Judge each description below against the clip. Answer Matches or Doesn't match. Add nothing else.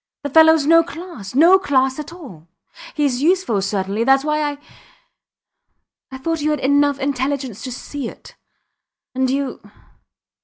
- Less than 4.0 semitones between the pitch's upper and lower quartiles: Matches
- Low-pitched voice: Doesn't match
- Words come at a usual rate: Matches